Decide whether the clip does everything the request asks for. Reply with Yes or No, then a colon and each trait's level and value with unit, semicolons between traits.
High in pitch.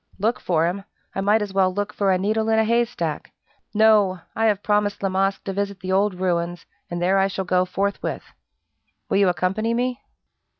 Yes: high, 195 Hz